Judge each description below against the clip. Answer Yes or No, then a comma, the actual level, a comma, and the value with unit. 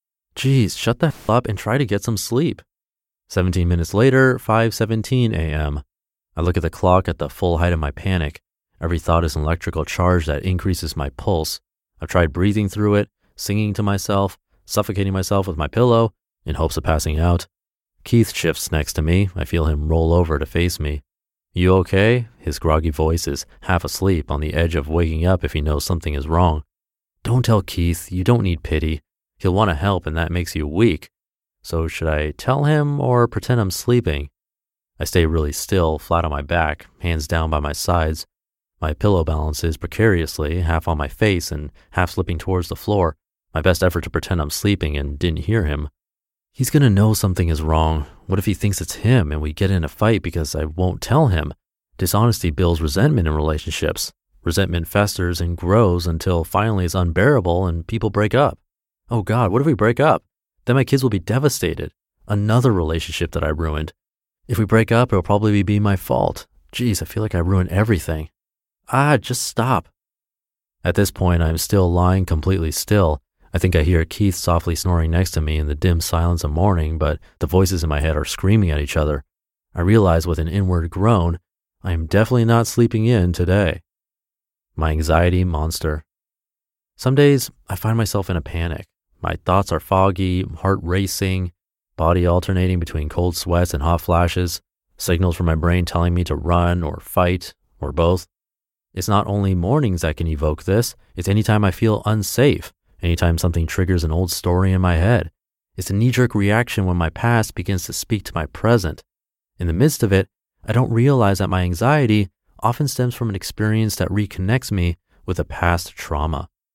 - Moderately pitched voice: No, very low, 90 Hz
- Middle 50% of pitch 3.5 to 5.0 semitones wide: Yes, average, 4.2 semitones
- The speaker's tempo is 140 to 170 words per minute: No, average, 195 wpm